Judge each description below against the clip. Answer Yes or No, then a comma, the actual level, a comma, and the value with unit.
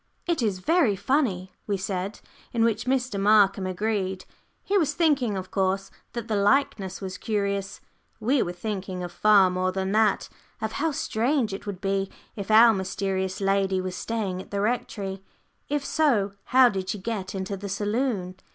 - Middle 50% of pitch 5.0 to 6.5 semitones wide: No, average, 3.3 semitones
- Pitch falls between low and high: No, high, 200 Hz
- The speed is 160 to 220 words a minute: Yes, average, 170 wpm